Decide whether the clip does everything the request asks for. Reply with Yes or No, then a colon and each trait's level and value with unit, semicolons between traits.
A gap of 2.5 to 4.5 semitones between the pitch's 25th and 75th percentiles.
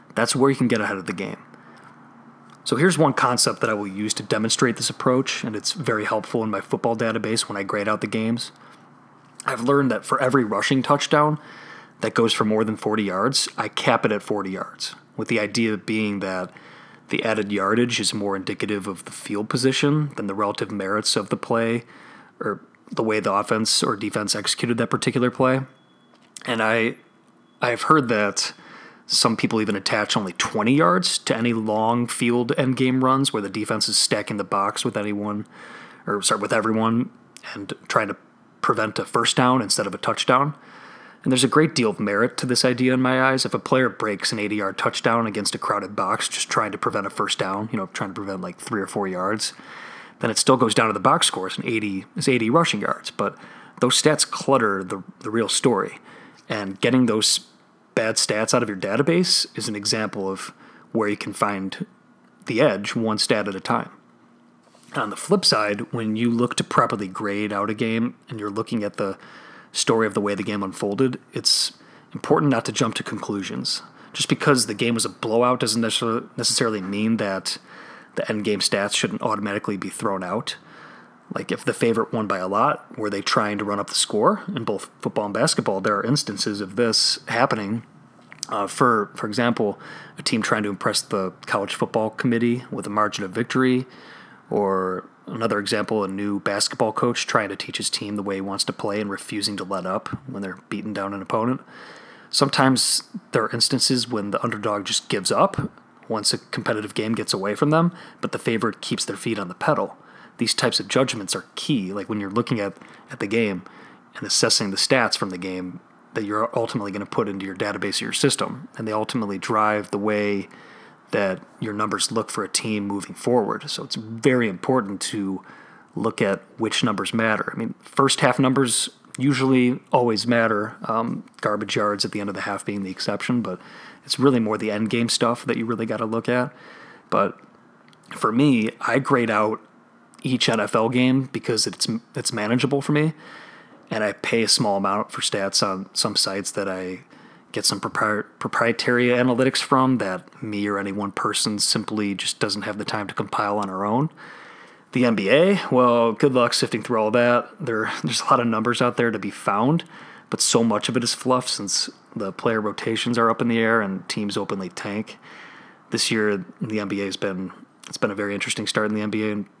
Yes: average, 3.3 semitones